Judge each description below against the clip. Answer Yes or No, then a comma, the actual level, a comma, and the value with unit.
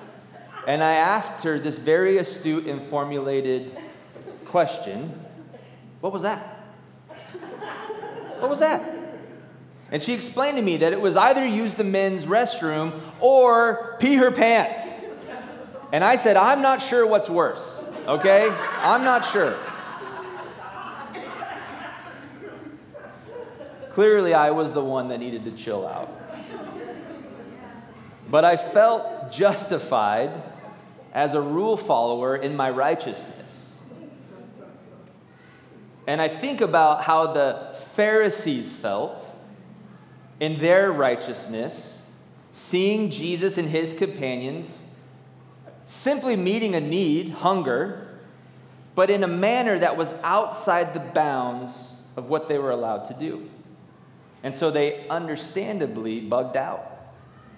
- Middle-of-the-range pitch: Yes, medium, 180 Hz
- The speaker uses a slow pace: Yes, slow, 115 wpm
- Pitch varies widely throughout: Yes, wide, 6.9 semitones